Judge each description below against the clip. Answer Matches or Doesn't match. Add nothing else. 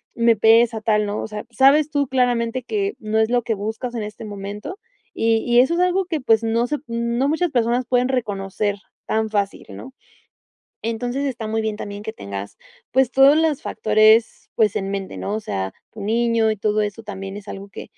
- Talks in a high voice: Matches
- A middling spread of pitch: Matches